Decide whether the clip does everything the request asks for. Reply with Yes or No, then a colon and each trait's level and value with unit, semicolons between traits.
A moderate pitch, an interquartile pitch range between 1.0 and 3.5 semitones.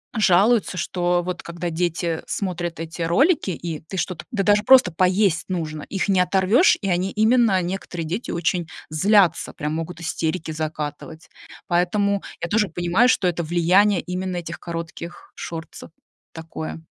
Yes: medium, 175 Hz; average, 2.9 semitones